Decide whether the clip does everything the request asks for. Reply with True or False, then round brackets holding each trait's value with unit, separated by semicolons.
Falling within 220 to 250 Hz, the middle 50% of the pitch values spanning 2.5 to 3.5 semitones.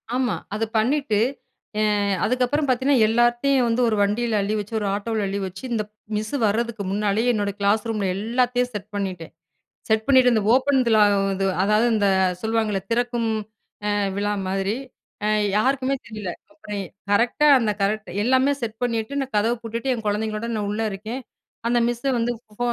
True (225 Hz; 2.9 semitones)